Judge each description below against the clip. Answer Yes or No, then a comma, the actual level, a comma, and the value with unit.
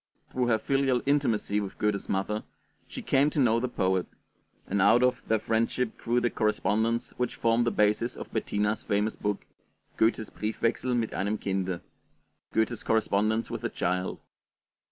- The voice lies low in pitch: Yes, low, 110 Hz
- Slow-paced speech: No, average, 155 wpm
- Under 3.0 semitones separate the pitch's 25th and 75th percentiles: Yes, narrow, 2.6 semitones